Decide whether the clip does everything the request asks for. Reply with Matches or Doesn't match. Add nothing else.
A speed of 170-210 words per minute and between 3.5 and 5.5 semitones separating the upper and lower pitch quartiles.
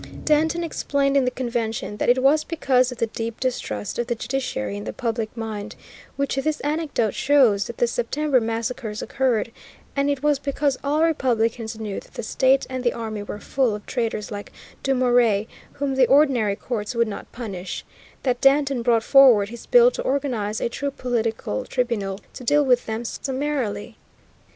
Matches